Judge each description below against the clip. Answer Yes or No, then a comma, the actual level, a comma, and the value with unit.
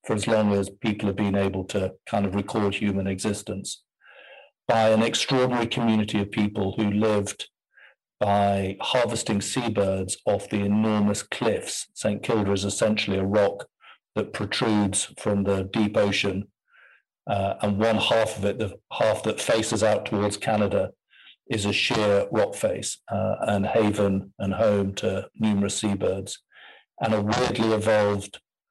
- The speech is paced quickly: No, average, 150 wpm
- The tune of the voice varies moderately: No, narrow, 1.6 semitones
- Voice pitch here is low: Yes, low, 105 Hz